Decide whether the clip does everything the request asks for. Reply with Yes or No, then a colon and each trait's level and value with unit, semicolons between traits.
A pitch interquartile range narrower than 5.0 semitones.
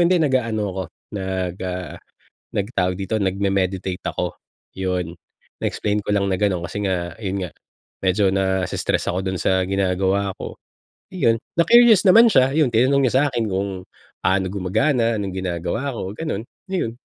Yes: average, 3.9 semitones